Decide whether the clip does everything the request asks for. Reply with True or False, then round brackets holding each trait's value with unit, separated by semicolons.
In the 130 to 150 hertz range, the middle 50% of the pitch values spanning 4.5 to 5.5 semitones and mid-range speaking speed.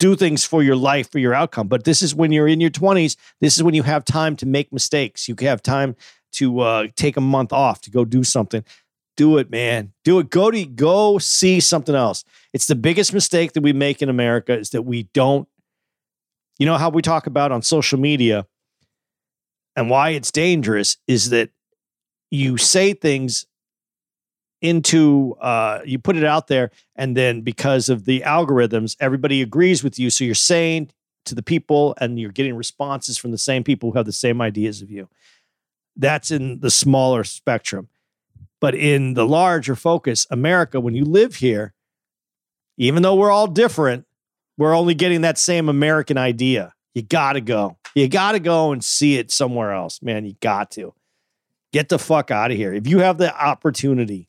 True (140 Hz; 4.8 semitones; 190 wpm)